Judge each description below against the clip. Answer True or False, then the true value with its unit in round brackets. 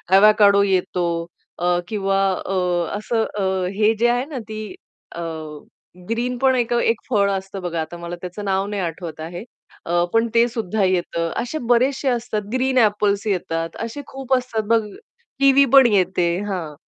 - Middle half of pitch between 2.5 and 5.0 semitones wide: True (4.6 semitones)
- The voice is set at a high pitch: True (210 Hz)